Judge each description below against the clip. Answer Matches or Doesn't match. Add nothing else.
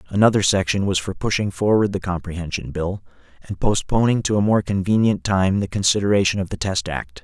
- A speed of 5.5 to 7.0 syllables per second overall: Matches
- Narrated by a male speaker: Matches